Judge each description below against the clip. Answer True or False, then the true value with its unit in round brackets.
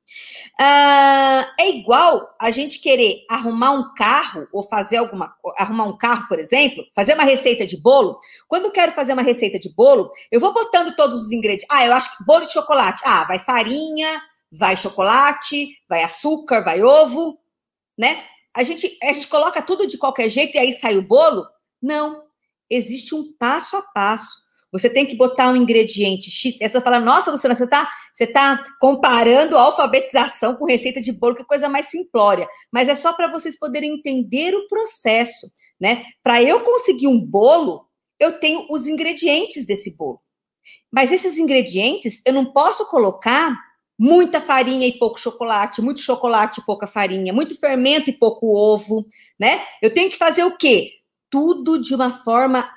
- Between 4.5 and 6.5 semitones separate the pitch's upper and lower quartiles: True (4.9 semitones)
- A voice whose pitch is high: True (270 Hz)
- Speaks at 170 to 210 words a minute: True (175 wpm)